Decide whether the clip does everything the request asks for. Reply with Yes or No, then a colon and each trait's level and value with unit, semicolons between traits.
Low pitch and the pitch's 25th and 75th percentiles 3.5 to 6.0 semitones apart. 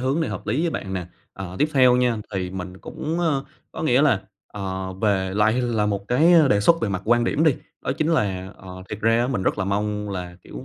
Yes: low, 105 Hz; wide, 5.4 semitones